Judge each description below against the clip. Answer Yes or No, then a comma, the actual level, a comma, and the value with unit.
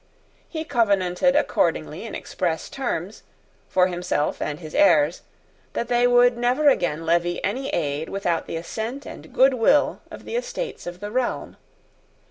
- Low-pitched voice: No, high, 200 Hz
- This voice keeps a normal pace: Yes, average, 145 wpm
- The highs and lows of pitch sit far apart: Yes, wide, 6.8 semitones